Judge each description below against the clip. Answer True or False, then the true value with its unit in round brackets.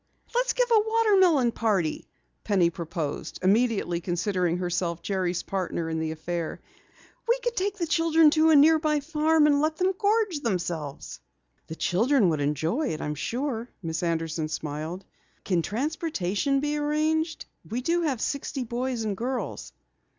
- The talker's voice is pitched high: True (235 Hz)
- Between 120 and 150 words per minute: True (145 wpm)